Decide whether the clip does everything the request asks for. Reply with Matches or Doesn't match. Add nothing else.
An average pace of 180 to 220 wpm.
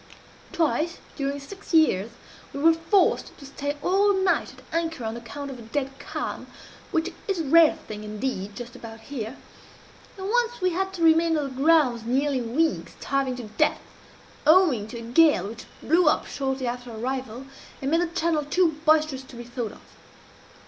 Matches